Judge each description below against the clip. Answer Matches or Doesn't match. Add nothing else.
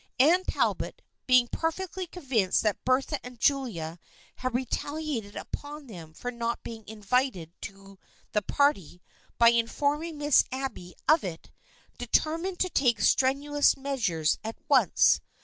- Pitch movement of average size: Doesn't match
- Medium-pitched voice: Doesn't match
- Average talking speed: Doesn't match